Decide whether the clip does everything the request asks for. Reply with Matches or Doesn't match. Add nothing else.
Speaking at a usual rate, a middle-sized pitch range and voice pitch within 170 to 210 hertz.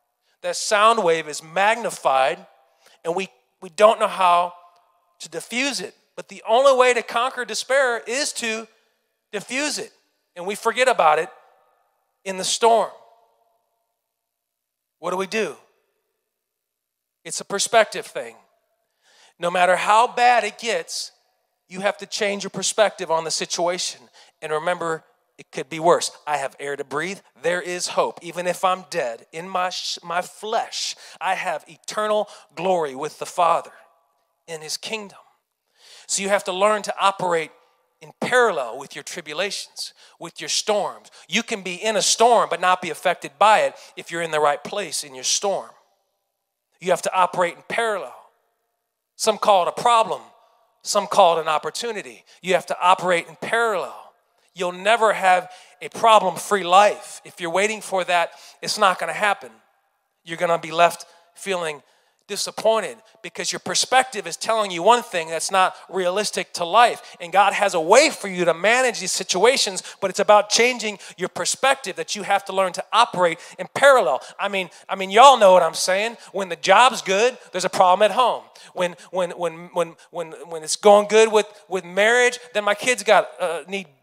Matches